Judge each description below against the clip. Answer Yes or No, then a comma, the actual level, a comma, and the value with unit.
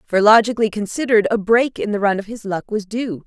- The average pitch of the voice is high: Yes, high, 215 Hz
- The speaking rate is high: Yes, fast, 240 wpm